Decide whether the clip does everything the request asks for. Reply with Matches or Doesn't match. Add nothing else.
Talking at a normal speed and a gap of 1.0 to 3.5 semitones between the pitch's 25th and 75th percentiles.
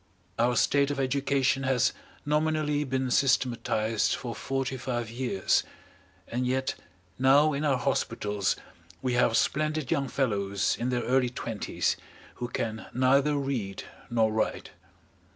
Doesn't match